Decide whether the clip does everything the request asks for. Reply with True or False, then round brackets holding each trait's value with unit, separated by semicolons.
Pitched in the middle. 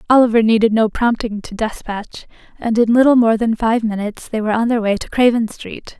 False (225 Hz)